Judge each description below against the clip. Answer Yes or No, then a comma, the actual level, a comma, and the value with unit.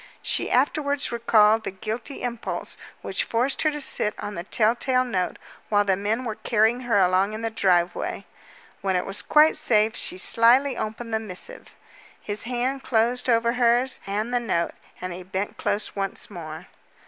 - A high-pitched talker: Yes, high, 225 Hz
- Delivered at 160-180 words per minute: Yes, average, 175 wpm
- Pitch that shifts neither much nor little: Yes, average, 3.7 semitones